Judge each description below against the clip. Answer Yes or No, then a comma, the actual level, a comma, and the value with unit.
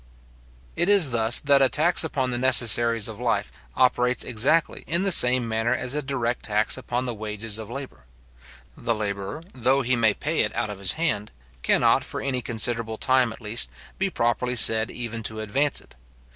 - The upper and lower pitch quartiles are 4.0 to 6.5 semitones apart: No, average, 3.0 semitones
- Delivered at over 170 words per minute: Yes, average, 185 wpm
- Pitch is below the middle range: Yes, low, 120 Hz